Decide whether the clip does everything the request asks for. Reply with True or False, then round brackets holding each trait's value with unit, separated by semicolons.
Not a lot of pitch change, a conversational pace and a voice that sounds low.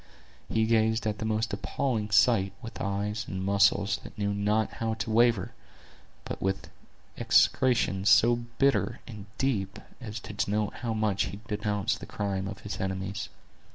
True (2.1 semitones; 155 wpm; 105 Hz)